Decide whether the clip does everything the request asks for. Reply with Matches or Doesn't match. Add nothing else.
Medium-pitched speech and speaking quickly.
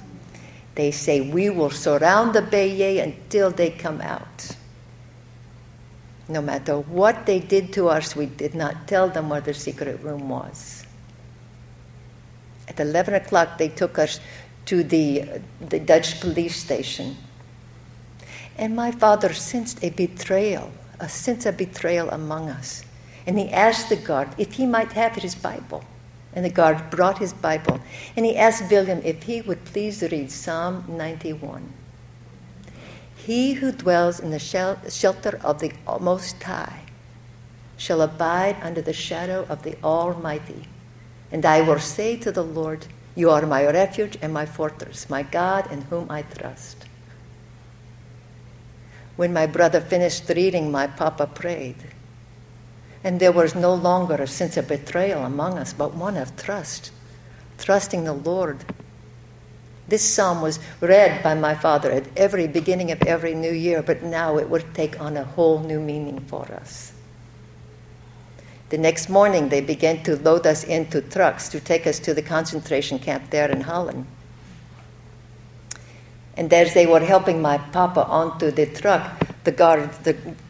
Doesn't match